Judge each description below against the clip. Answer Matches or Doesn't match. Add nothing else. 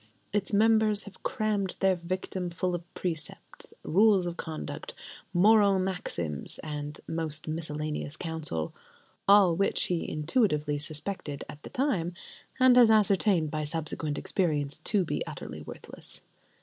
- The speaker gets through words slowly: Matches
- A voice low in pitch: Doesn't match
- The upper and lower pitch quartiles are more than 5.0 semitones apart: Doesn't match